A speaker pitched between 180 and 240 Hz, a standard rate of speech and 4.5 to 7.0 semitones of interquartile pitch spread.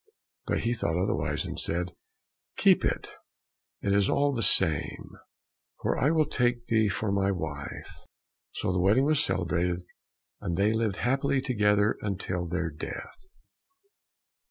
No: low, 100 Hz; average, 145 wpm; average, 5.1 semitones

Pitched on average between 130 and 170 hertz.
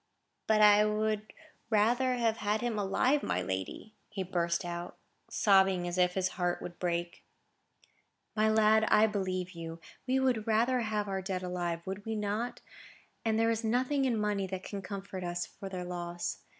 No: high, 205 Hz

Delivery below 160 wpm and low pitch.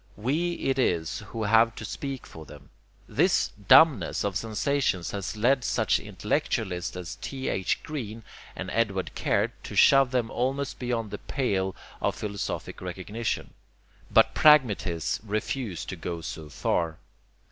Yes: slow, 135 wpm; low, 110 Hz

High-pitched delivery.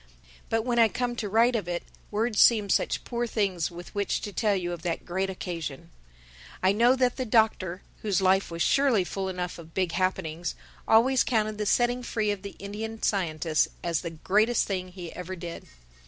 Yes: high, 195 Hz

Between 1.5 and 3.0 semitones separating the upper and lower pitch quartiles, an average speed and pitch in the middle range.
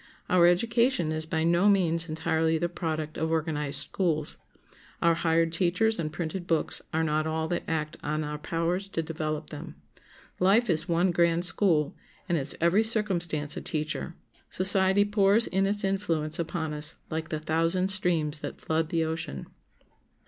Yes: narrow, 2.6 semitones; average, 165 wpm; medium, 165 Hz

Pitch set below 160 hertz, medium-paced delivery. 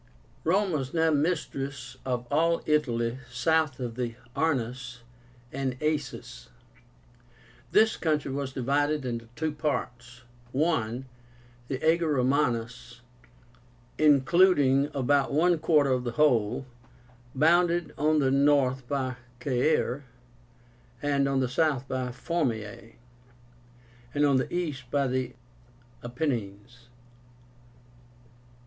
No: low, 135 Hz; slow, 105 wpm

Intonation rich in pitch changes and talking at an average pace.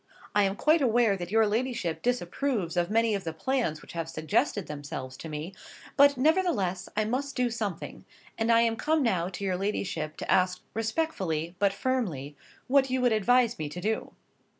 Yes: wide, 6.3 semitones; average, 185 wpm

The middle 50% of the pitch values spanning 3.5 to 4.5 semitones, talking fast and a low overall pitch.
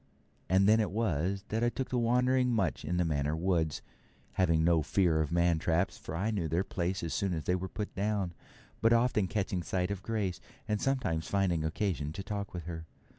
Yes: average, 4.2 semitones; fast, 210 wpm; very low, 95 Hz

